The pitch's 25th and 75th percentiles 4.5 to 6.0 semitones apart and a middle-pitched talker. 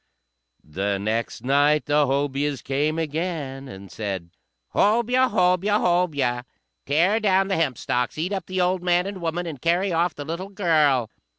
Yes: average, 5.2 semitones; medium, 160 Hz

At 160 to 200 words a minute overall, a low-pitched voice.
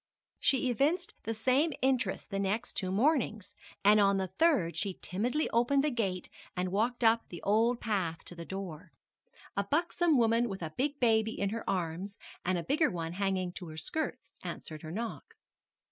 No: average, 180 wpm; high, 215 Hz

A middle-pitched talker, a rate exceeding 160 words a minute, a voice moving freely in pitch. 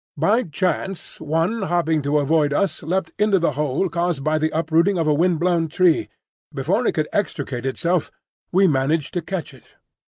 No: medium, 165 Hz; average, 180 wpm; average, 3.3 semitones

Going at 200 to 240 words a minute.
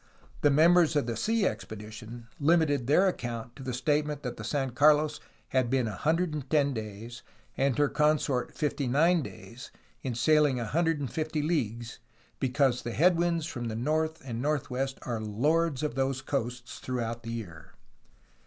No: average, 155 wpm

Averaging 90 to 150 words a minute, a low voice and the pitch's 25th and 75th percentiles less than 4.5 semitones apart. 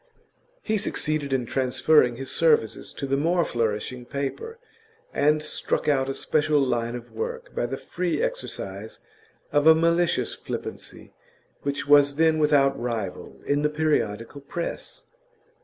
No: average, 140 wpm; medium, 145 Hz; average, 3.5 semitones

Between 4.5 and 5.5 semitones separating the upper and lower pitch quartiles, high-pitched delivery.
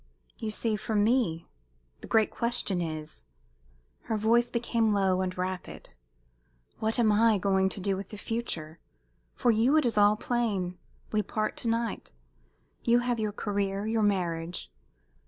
No: average, 3.6 semitones; high, 210 Hz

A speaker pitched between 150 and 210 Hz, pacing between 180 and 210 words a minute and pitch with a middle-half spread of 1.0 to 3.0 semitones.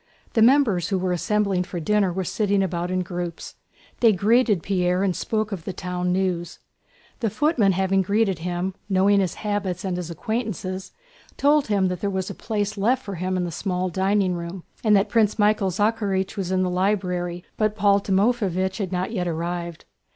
Yes: high, 190 Hz; average, 185 wpm; narrow, 2.5 semitones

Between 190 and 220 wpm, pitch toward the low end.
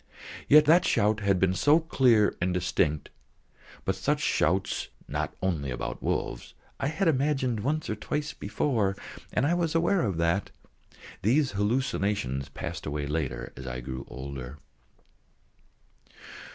No: average, 140 wpm; low, 100 Hz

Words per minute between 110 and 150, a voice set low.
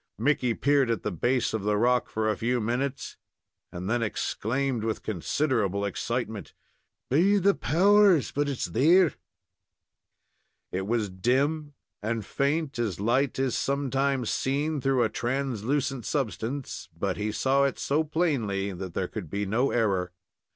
Yes: average, 145 wpm; low, 125 Hz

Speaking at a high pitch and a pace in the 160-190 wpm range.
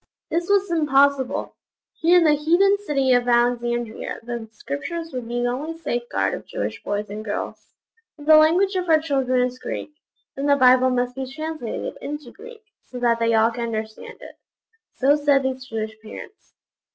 Yes: very high, 260 Hz; average, 175 wpm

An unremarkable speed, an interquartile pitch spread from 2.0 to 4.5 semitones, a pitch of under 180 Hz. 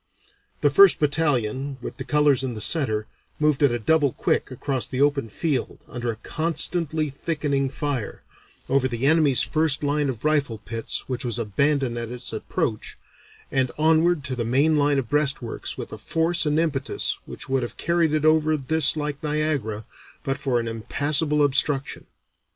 Yes: average, 170 wpm; average, 3.6 semitones; medium, 140 Hz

